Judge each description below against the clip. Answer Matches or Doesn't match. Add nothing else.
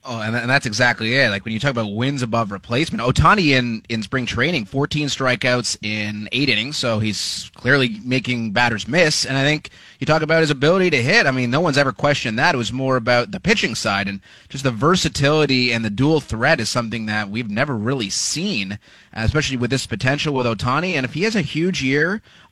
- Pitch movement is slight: Doesn't match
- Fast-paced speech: Matches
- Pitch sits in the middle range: Doesn't match